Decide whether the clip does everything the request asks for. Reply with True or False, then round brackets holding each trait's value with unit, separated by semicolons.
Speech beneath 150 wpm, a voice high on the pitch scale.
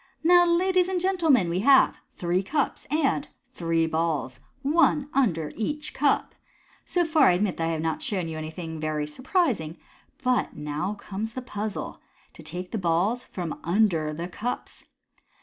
False (160 wpm; 205 Hz)